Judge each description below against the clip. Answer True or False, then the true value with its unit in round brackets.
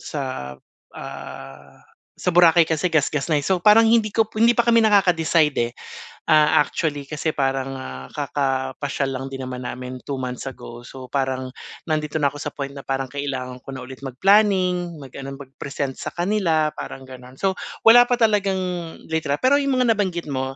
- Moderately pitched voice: True (145 Hz)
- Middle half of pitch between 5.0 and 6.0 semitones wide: True (5.4 semitones)